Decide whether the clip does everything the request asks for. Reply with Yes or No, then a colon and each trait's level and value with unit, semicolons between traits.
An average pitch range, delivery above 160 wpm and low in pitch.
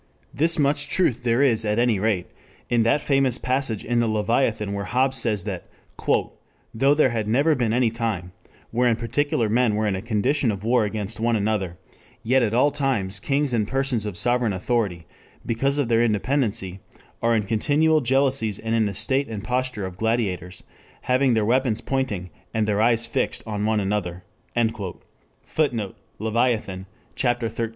Yes: average, 3.6 semitones; average, 170 wpm; low, 115 Hz